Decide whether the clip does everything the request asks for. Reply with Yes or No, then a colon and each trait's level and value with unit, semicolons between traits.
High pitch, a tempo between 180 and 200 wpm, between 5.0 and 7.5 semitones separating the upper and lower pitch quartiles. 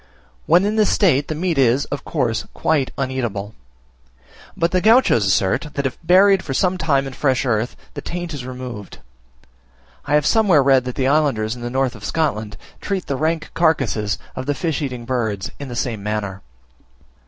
No: low, 135 Hz; average, 185 wpm; average, 5.3 semitones